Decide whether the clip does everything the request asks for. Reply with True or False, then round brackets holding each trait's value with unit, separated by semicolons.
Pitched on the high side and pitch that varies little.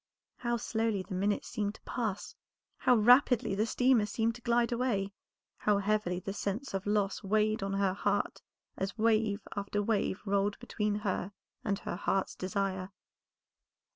True (205 Hz; 2.3 semitones)